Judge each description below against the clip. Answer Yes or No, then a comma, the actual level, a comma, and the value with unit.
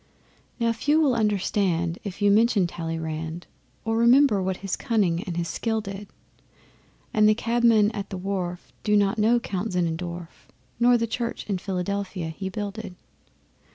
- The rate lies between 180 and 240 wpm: No, average, 155 wpm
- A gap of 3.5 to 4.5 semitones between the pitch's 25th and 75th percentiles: Yes, average, 3.9 semitones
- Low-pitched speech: No, high, 200 Hz